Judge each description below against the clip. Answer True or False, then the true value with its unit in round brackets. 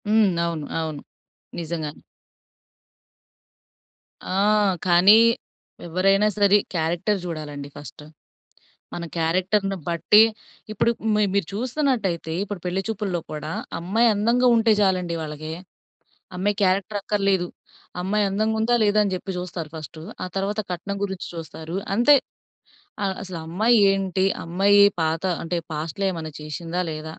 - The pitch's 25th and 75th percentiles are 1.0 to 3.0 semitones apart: False (3.8 semitones)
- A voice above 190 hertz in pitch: False (185 Hz)